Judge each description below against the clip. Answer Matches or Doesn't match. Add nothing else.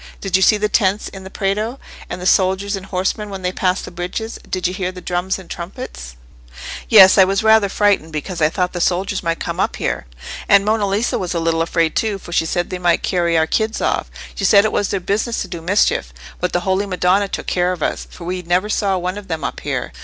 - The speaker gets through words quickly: Matches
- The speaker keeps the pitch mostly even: Matches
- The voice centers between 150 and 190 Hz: Matches